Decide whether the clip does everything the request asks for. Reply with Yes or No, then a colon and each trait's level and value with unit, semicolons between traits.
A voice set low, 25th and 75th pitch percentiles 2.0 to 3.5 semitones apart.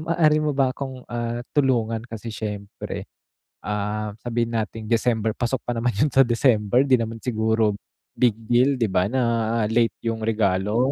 Yes: low, 115 Hz; average, 2.7 semitones